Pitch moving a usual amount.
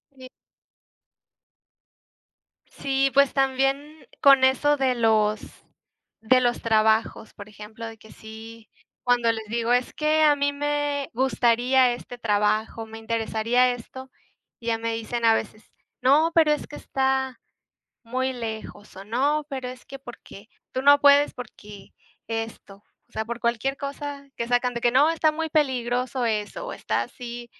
Yes: average, 3.4 semitones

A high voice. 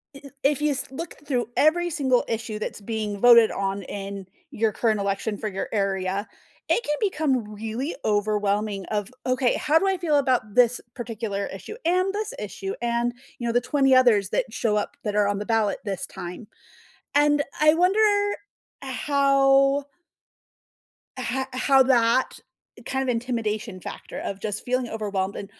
Yes: high, 235 Hz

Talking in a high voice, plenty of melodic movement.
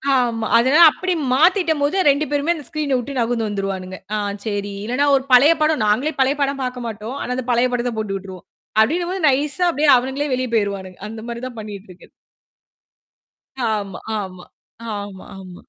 Yes: high, 245 Hz; wide, 5.7 semitones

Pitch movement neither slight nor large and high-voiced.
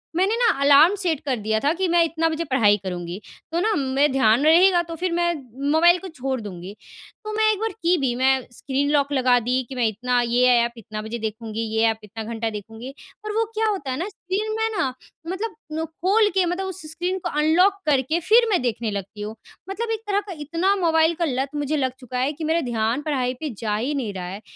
No: wide, 7.0 semitones; very high, 285 Hz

